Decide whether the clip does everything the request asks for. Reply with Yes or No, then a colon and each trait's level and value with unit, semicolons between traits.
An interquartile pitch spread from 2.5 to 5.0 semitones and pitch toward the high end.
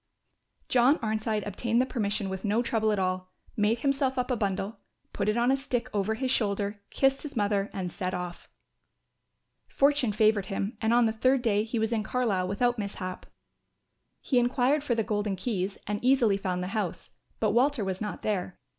Yes: average, 3.5 semitones; high, 215 Hz